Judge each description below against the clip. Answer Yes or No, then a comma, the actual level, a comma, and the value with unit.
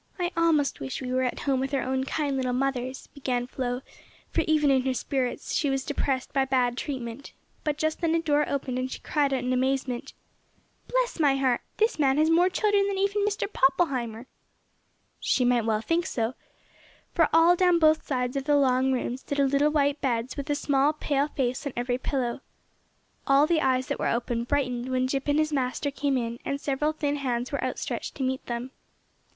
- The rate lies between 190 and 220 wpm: Yes, average, 200 wpm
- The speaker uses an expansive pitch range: No, average, 2.8 semitones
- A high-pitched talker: Yes, very high, 270 Hz